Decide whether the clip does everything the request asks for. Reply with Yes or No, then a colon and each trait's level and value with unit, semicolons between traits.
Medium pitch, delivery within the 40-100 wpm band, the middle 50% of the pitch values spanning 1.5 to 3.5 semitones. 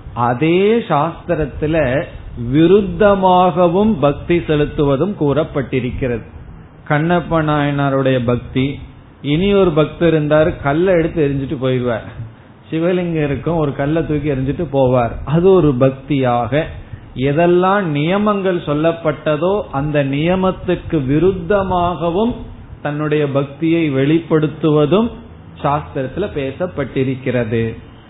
No: medium, 150 Hz; slow, 75 wpm; average, 4.3 semitones